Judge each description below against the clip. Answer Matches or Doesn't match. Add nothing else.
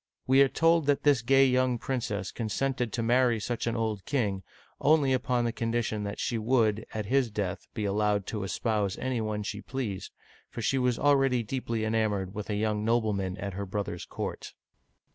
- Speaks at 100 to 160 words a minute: Doesn't match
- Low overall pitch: Matches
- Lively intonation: Doesn't match